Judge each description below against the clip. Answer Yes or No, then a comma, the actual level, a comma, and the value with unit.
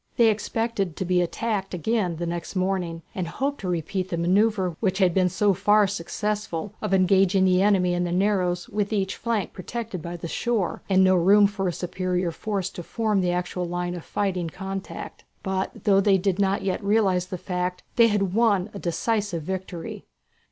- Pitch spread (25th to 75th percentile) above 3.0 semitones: No, narrow, 2.5 semitones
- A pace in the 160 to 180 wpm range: No, average, 190 wpm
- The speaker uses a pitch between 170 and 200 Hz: Yes, high, 190 Hz